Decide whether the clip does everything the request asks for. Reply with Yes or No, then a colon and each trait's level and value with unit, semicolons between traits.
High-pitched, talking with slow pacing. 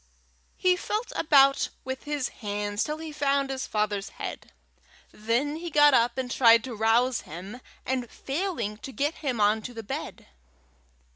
No: very high, 255 Hz; average, 160 wpm